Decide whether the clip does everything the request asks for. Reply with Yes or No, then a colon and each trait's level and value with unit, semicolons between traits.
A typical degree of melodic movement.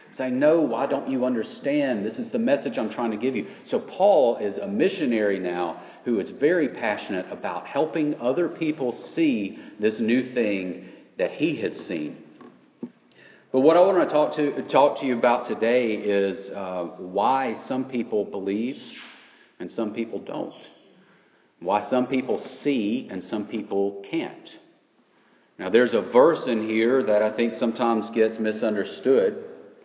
Yes: average, 4.6 semitones